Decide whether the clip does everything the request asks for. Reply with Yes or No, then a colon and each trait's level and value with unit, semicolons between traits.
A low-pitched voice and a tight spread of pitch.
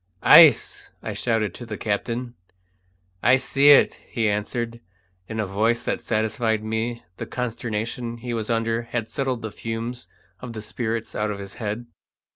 Yes: low, 115 Hz; narrow, 1.7 semitones